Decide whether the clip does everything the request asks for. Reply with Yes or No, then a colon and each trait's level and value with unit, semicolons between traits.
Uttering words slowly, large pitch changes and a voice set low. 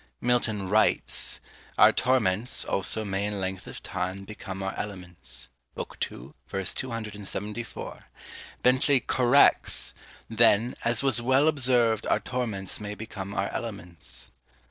No: slow, 120 wpm; average, 4.0 semitones; low, 110 Hz